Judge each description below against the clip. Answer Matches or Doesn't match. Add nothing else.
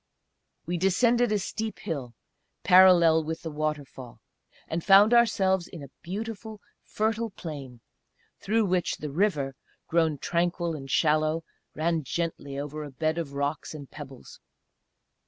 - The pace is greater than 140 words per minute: Doesn't match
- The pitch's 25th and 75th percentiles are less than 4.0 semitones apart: Doesn't match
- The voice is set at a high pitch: Doesn't match